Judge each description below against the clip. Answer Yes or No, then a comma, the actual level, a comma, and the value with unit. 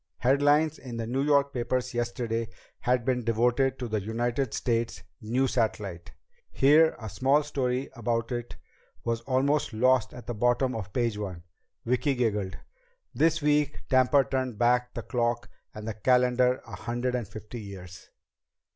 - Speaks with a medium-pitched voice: No, low, 120 Hz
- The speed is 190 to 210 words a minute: No, average, 155 wpm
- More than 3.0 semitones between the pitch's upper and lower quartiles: No, narrow, 2.5 semitones